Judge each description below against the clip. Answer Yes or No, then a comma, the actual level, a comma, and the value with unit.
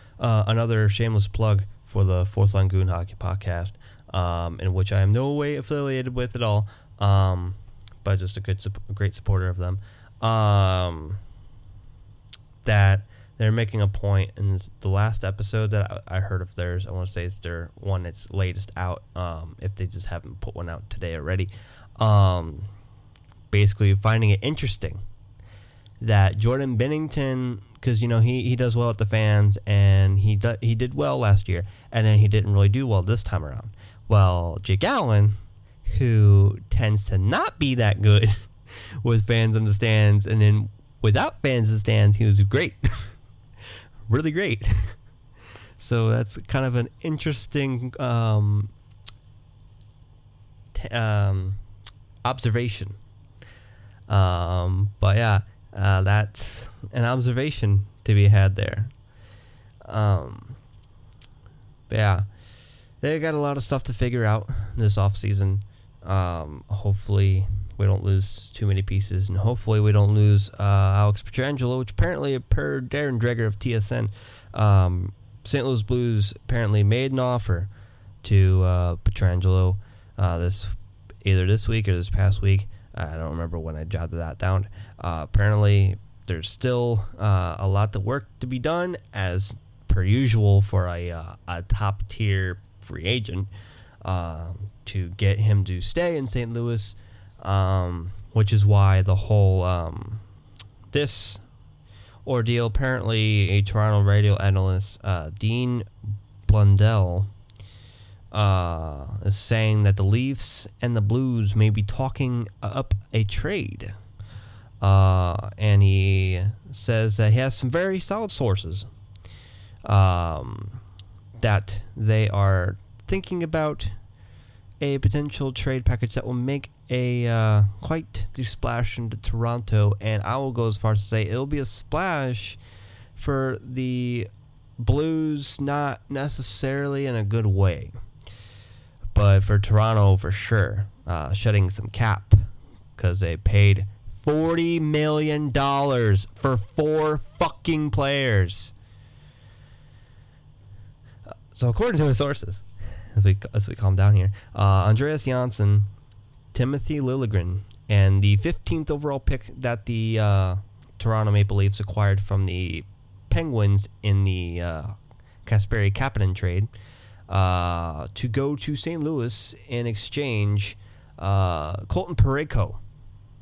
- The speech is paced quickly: No, average, 140 wpm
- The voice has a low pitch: Yes, low, 105 Hz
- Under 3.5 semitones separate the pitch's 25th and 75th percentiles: Yes, average, 2.9 semitones